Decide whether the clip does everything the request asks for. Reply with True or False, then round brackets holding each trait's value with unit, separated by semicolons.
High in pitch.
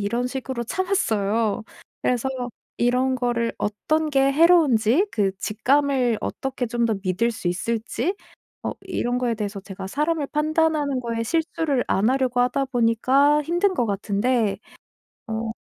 True (245 Hz)